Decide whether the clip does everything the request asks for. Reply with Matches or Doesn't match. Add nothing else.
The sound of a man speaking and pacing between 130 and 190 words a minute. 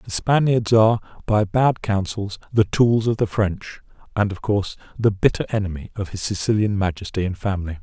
Matches